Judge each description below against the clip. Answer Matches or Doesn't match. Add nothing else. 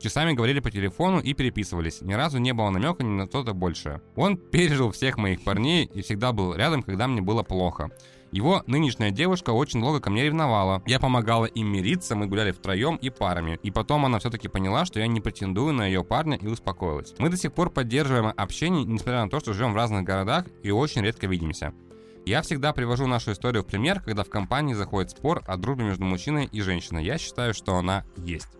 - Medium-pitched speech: Doesn't match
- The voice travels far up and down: Matches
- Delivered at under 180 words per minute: Doesn't match